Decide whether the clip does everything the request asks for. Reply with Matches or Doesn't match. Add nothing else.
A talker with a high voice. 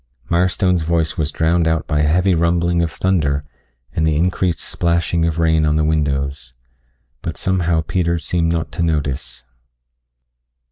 Doesn't match